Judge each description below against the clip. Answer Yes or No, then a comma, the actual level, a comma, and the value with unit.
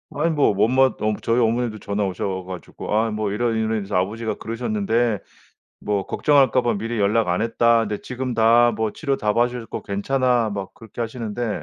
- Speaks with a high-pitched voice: No, low, 115 Hz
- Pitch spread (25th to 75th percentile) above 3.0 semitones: No, narrow, 2.5 semitones